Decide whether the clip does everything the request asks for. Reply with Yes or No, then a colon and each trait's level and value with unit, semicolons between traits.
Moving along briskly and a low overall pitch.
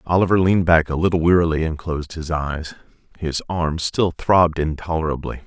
No: average, 165 wpm; very low, 80 Hz